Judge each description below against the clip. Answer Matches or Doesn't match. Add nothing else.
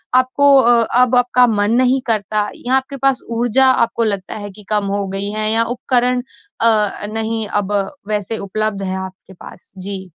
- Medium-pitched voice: Doesn't match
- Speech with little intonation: Doesn't match